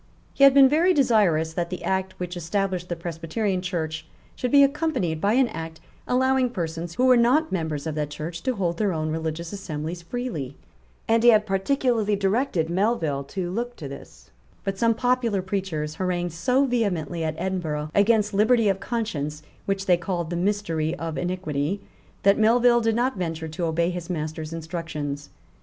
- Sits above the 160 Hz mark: Yes, medium, 185 Hz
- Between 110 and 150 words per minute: No, average, 175 wpm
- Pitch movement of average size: No, wide, 5.8 semitones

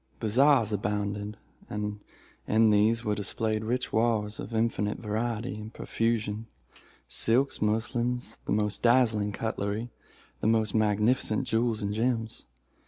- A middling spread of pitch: No, narrow, 1.9 semitones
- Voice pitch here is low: Yes, low, 110 Hz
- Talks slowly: Yes, slow, 115 wpm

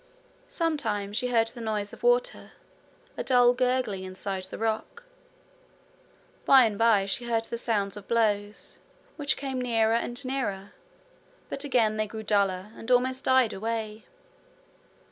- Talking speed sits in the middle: Yes, average, 145 wpm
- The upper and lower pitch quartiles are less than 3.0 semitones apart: No, average, 3.5 semitones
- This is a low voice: No, high, 225 Hz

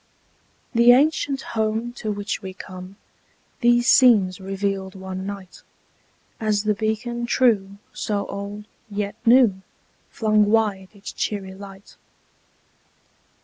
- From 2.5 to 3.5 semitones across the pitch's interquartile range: Yes, average, 2.9 semitones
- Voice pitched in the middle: No, high, 205 Hz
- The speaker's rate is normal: No, slow, 110 wpm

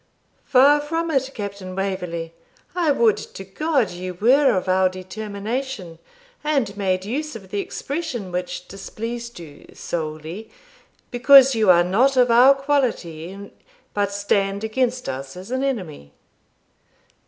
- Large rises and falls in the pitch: Yes, wide, 6.1 semitones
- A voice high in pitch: Yes, high, 205 Hz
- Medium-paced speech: No, slow, 130 wpm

